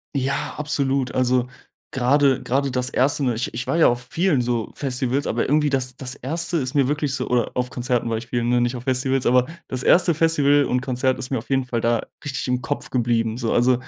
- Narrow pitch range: Yes, narrow, 2.2 semitones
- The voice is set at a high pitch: No, low, 130 Hz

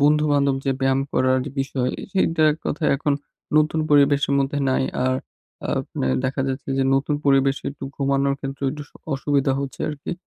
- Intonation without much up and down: Yes, narrow, 1.5 semitones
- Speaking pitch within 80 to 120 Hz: No, medium, 140 Hz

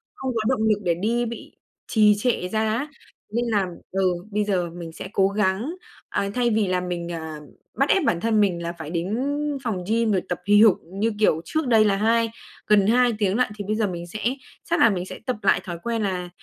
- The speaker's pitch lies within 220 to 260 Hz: No, high, 205 Hz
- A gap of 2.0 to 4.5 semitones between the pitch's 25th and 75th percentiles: Yes, average, 3.9 semitones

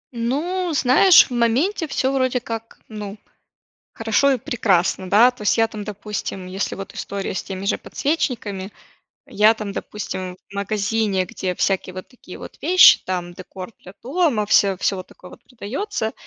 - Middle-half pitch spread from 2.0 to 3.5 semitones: No, average, 4.5 semitones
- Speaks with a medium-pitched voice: No, high, 215 Hz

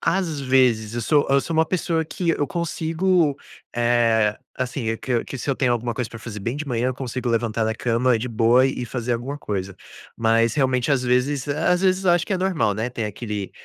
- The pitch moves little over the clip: No, average, 4.5 semitones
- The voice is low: Yes, low, 125 Hz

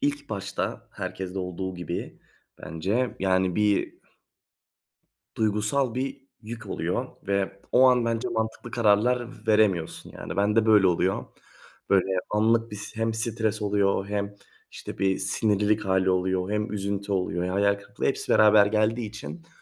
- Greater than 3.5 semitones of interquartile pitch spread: No, average, 2.7 semitones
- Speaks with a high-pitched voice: No, low, 105 Hz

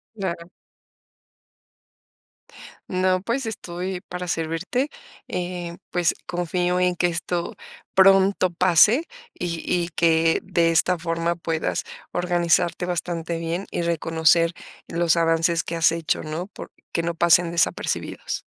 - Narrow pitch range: Yes, narrow, 1.4 semitones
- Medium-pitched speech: Yes, medium, 175 Hz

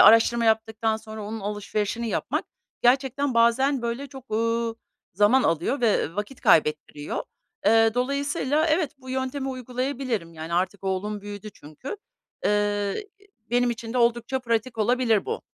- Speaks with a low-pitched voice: No, high, 230 Hz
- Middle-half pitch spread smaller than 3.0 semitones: No, average, 3.8 semitones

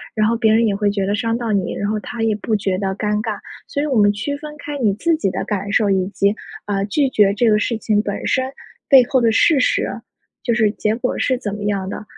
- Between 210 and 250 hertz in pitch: Yes, high, 215 Hz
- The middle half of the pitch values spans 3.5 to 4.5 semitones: No, average, 3.0 semitones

